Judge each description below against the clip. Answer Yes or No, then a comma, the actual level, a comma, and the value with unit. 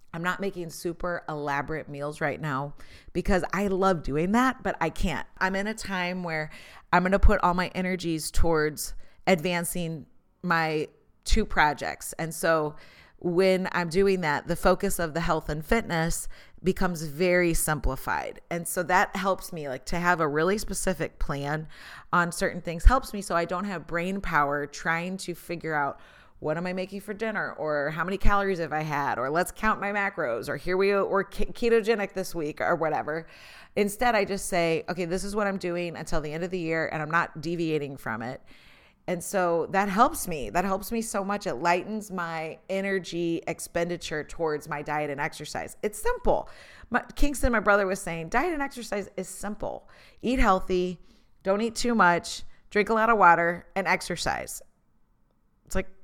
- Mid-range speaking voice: Yes, medium, 180 Hz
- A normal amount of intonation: Yes, average, 3.3 semitones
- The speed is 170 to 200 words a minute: Yes, average, 185 wpm